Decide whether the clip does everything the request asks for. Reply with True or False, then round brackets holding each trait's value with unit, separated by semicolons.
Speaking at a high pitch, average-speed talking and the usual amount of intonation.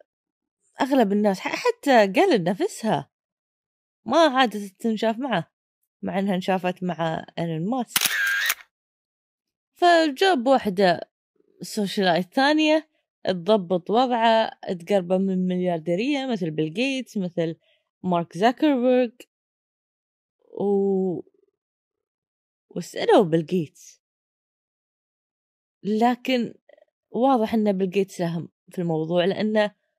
False (210 Hz; 80 wpm; 6.8 semitones)